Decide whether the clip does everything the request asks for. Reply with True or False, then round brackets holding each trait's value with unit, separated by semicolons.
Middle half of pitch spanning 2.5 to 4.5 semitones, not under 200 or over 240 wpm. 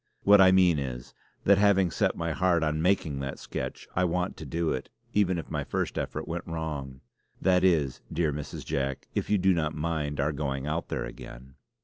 True (4.1 semitones; 205 wpm)